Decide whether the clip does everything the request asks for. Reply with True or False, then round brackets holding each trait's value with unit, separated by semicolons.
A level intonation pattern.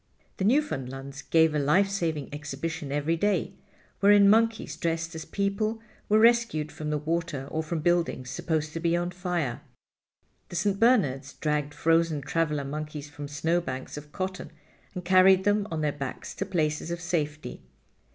False (4.0 semitones)